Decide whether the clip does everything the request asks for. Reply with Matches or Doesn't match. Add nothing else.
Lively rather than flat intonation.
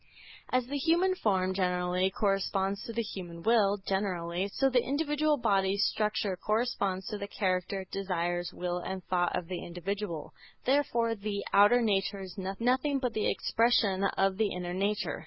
Doesn't match